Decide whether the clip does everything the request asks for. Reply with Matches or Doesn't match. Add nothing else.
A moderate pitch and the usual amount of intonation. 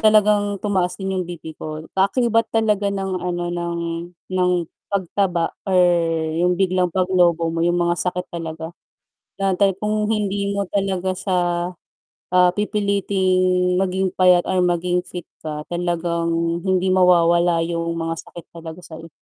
Doesn't match